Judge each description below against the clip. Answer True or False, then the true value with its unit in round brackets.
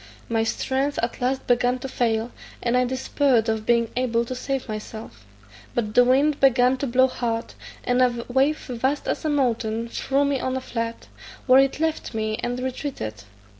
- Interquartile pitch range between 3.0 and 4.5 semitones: False (2.4 semitones)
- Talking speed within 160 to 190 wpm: True (180 wpm)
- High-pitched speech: True (250 Hz)